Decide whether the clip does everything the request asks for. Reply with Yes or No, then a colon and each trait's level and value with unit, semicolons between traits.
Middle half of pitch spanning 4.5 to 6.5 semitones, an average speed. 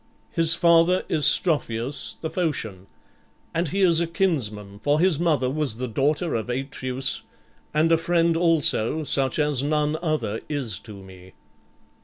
Yes: average, 5.1 semitones; average, 150 wpm